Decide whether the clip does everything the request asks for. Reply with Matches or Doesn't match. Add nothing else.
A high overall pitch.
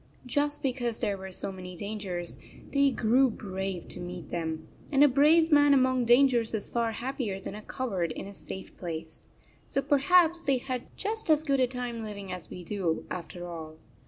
Matches